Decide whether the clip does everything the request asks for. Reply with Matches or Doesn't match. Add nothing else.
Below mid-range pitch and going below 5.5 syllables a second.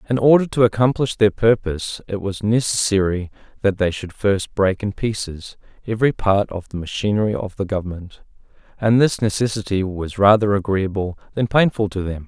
Matches